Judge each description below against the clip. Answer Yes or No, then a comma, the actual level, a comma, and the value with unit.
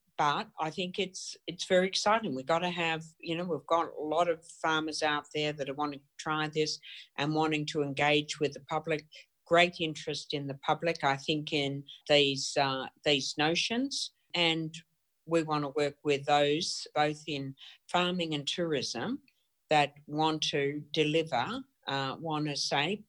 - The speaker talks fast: No, average, 170 wpm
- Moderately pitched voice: Yes, medium, 155 Hz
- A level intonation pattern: Yes, narrow, 2.3 semitones